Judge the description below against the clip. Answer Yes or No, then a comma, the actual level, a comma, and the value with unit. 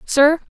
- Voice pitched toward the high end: Yes, very high, 300 Hz